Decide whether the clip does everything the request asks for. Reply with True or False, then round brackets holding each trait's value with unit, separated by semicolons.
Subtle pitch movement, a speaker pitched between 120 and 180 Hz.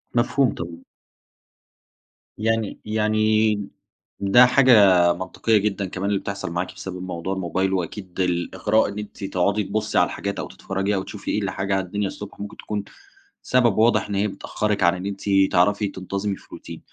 False (2.2 semitones; 100 Hz)